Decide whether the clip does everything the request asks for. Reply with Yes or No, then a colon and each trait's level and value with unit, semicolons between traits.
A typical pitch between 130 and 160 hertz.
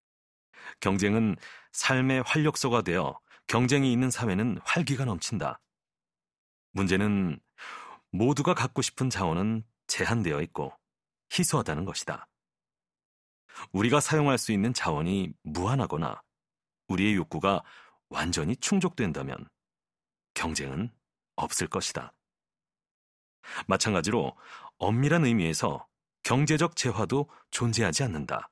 No: low, 120 Hz